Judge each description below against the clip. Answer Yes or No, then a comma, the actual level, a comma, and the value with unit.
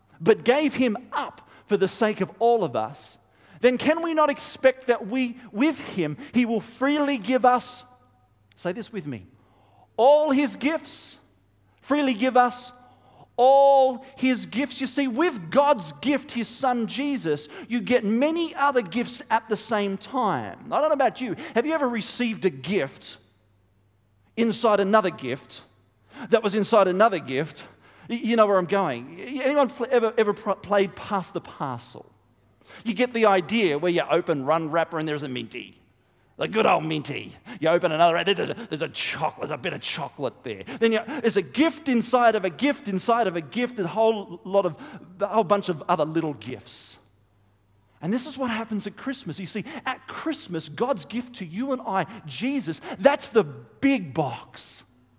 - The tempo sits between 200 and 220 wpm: No, average, 175 wpm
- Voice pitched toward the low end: No, high, 215 Hz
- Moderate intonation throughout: No, wide, 8.2 semitones